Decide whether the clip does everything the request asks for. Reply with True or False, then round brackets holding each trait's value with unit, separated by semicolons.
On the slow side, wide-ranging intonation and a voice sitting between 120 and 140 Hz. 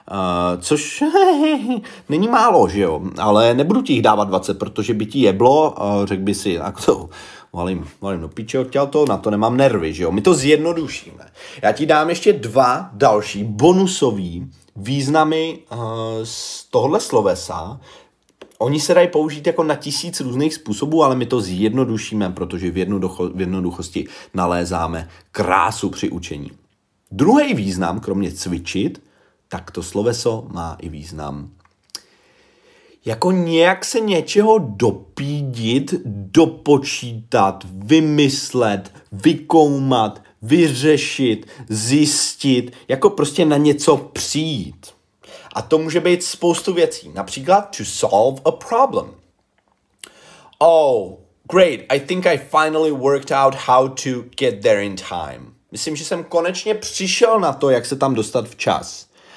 False (135 wpm; 8.1 semitones; 135 Hz)